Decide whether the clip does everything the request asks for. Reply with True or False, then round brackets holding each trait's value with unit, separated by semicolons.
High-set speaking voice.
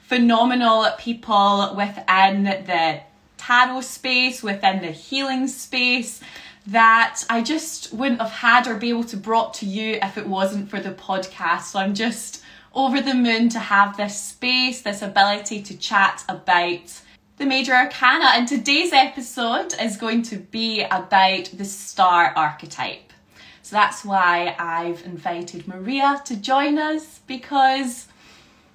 True (225 Hz)